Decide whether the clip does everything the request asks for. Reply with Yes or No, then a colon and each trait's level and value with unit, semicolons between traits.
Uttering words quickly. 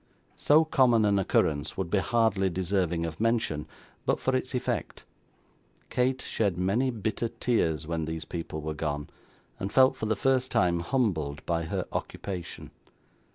No: average, 155 wpm